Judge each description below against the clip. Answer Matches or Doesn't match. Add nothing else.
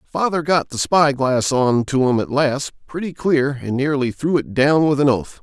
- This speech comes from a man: Matches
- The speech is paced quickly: Matches